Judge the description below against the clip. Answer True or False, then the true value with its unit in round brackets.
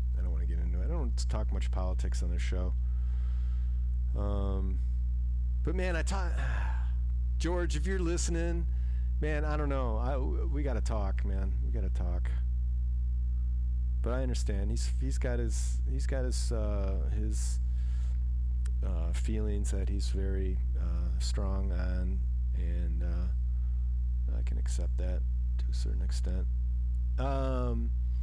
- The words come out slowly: True (130 wpm)